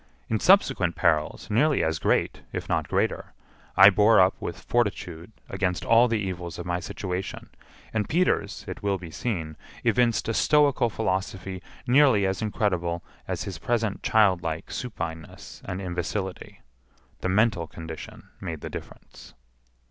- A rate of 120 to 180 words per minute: Yes, average, 140 wpm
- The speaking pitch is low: Yes, very low, 95 Hz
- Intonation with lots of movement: No, average, 4.5 semitones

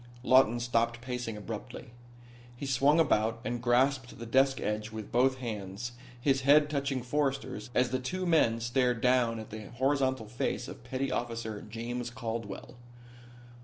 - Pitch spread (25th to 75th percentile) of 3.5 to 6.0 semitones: No, narrow, 2.5 semitones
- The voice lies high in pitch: No, low, 120 Hz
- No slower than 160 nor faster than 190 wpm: No, average, 150 wpm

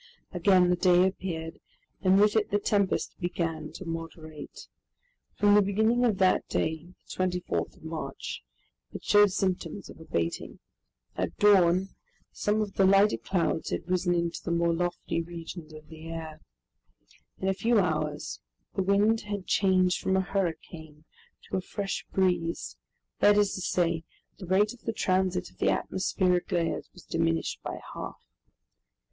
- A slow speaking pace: No, average, 155 wpm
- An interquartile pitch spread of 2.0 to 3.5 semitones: Yes, average, 2.9 semitones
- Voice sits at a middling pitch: Yes, medium, 180 Hz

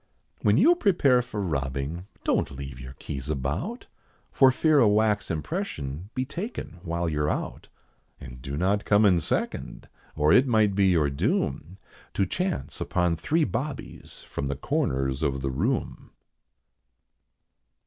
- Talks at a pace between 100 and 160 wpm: Yes, average, 145 wpm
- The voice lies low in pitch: Yes, very low, 90 Hz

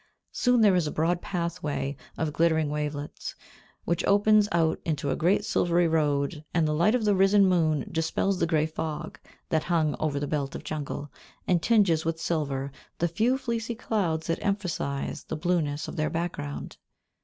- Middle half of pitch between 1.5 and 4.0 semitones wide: Yes, average, 3.4 semitones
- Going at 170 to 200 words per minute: Yes, average, 175 wpm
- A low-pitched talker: No, medium, 165 Hz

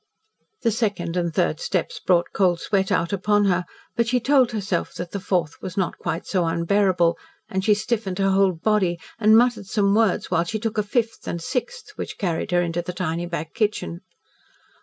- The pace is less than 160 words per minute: No, average, 195 wpm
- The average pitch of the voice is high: Yes, high, 195 Hz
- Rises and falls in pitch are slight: No, average, 3.8 semitones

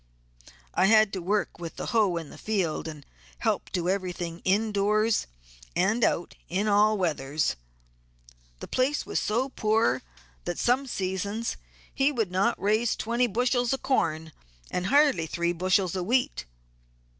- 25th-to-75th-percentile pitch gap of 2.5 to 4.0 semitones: No, average, 4.6 semitones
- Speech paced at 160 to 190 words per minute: No, average, 150 wpm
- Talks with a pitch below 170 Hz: No, high, 200 Hz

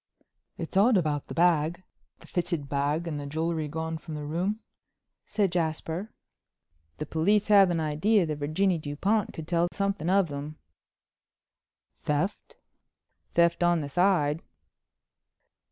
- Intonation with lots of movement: No, average, 3.7 semitones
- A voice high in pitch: No, medium, 165 Hz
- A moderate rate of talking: No, slow, 130 wpm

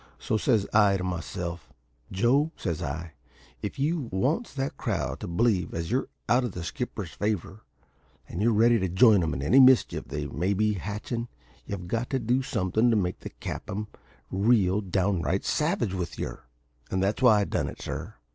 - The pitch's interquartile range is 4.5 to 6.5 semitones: Yes, average, 4.9 semitones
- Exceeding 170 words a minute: Yes, average, 185 wpm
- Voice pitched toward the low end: Yes, low, 105 Hz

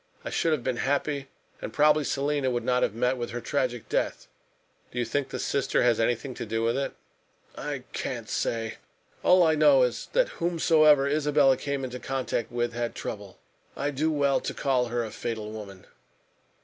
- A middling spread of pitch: Yes, average, 3.4 semitones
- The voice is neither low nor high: No, low, 130 Hz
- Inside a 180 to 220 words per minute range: Yes, average, 190 wpm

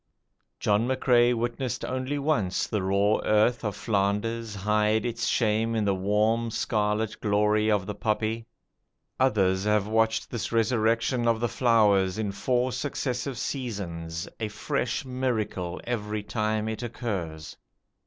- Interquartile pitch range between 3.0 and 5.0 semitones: No, narrow, 2.4 semitones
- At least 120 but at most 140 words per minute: Yes, slow, 135 wpm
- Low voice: Yes, low, 110 Hz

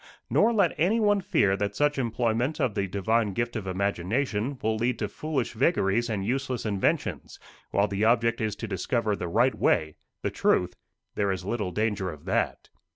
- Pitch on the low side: Yes, low, 110 Hz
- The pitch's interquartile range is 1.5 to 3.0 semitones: No, average, 4.2 semitones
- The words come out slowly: No, average, 175 wpm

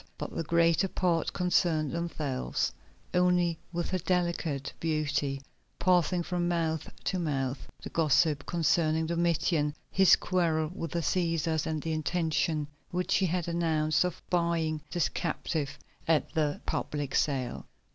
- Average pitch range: No, narrow, 2.2 semitones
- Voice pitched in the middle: Yes, medium, 165 Hz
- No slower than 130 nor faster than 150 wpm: Yes, slow, 135 wpm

